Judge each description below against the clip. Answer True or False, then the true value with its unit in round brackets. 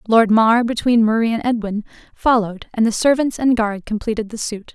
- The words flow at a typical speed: True (190 wpm)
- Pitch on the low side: False (225 Hz)